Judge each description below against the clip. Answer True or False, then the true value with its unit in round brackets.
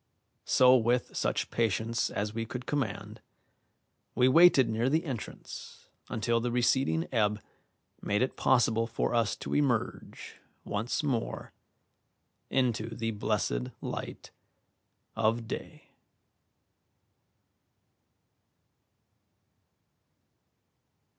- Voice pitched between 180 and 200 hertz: False (115 Hz)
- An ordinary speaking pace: False (90 wpm)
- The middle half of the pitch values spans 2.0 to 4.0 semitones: True (2.4 semitones)